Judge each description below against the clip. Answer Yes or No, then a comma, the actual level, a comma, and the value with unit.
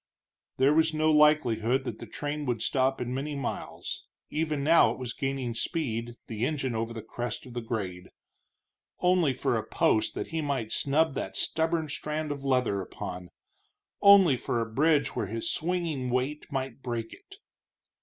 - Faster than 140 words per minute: Yes, average, 170 wpm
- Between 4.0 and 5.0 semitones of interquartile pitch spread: Yes, average, 4.5 semitones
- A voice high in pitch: No, low, 135 Hz